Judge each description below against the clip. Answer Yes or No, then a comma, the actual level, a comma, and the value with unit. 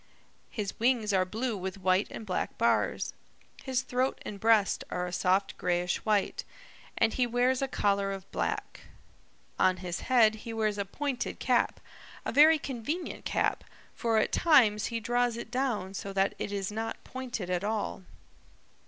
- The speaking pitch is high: Yes, high, 215 Hz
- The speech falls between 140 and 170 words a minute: Yes, average, 165 wpm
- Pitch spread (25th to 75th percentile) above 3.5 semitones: Yes, average, 4.0 semitones